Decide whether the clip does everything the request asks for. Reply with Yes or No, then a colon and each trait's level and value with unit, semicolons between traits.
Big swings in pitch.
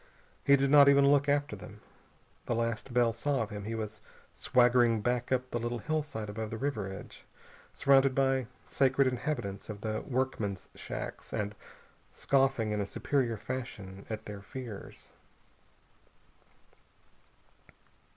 No: average, 3.8 semitones